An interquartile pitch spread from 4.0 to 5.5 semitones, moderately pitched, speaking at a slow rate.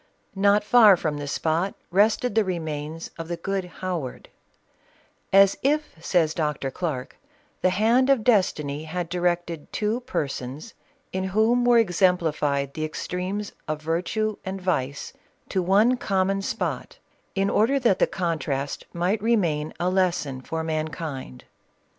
No: average, 4.6 semitones; medium, 180 Hz; average, 145 wpm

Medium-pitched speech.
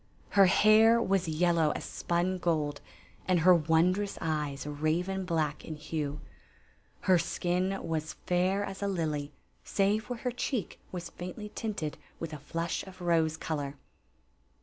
Yes: medium, 175 Hz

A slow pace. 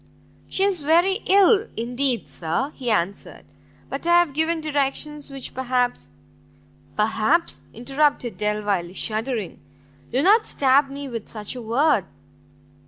Yes: slow, 130 wpm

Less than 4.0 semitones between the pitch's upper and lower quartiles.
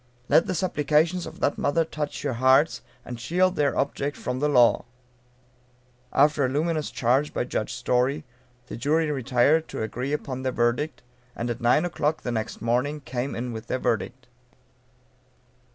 Yes: average, 3.6 semitones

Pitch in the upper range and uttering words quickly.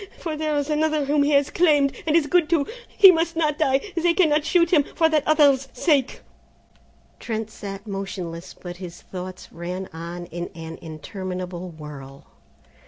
No: very high, 270 Hz; average, 170 wpm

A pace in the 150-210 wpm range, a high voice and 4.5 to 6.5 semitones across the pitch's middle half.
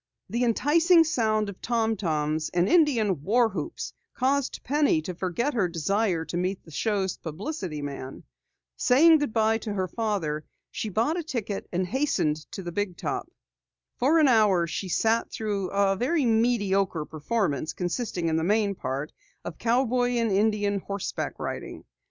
Yes: average, 155 wpm; high, 205 Hz; average, 5.3 semitones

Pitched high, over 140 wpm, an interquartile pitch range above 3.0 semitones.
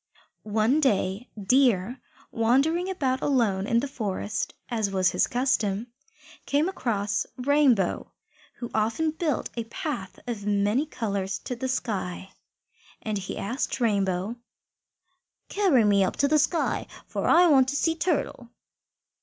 No: high, 235 Hz; slow, 135 wpm; wide, 5.6 semitones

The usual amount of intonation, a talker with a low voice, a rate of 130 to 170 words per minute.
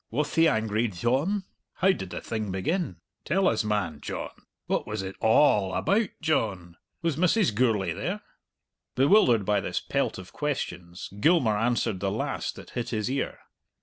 No: wide, 7.9 semitones; low, 115 Hz; average, 165 wpm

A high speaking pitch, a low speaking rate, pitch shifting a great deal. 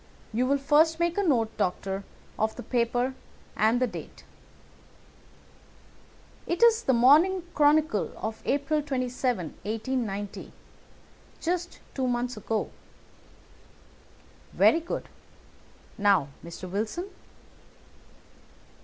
Yes: very high, 255 Hz; slow, 100 wpm; wide, 5.9 semitones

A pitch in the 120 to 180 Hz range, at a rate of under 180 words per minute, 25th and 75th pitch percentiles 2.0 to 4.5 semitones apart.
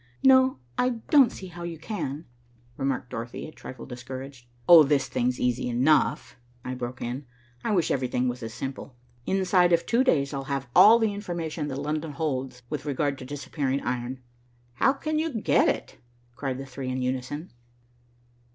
No: medium, 140 Hz; average, 170 wpm; average, 5.1 semitones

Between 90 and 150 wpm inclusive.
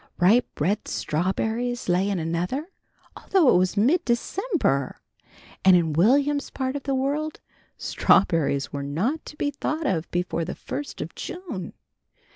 Yes: average, 145 wpm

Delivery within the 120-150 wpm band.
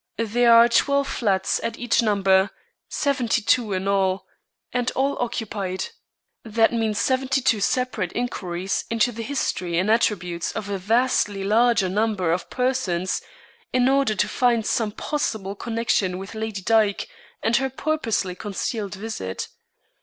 Yes: average, 140 wpm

